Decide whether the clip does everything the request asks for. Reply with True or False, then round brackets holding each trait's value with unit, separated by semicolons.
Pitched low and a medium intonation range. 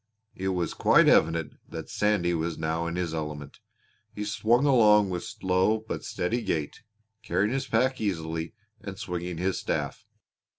True (90 Hz; 4.2 semitones)